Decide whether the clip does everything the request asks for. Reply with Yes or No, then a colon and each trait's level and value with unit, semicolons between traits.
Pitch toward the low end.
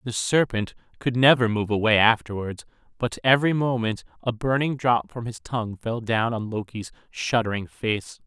Yes: low, 115 Hz